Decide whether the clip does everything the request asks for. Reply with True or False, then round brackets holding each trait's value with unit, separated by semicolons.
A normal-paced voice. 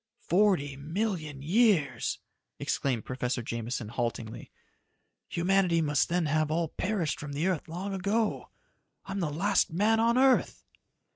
False (130 wpm)